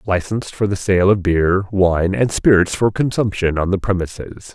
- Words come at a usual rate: Yes, average, 185 wpm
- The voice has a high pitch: No, very low, 95 Hz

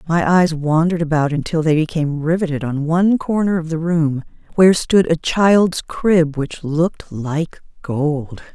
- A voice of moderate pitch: Yes, medium, 160 Hz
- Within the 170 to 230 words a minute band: No, average, 160 wpm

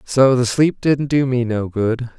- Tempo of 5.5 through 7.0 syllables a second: No, 3.9 syllables/s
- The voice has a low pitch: Yes, low, 125 Hz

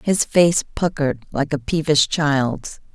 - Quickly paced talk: No, average, 145 wpm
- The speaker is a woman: Yes, female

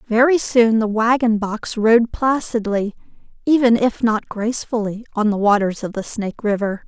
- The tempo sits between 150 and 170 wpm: Yes, average, 155 wpm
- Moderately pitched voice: No, high, 225 Hz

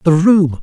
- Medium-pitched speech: Yes, medium, 170 Hz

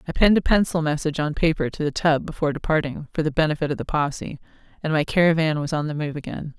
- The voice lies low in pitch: No, medium, 155 Hz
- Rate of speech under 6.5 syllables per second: No, 7.1 syllables/s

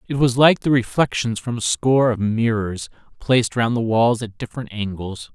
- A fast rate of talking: No, average, 190 wpm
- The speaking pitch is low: Yes, low, 115 Hz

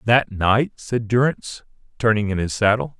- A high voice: No, low, 110 Hz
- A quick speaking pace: No, average, 160 wpm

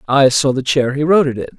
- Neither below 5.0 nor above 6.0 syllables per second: No, 6.8 syllables/s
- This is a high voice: No, medium, 140 Hz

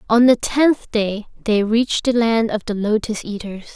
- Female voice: Yes, female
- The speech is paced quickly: No, average, 190 wpm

